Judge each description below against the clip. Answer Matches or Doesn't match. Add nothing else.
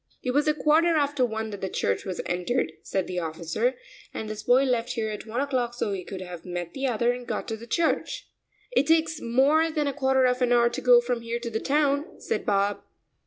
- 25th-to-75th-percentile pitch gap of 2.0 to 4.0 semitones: Doesn't match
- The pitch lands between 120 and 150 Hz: Doesn't match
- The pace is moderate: Doesn't match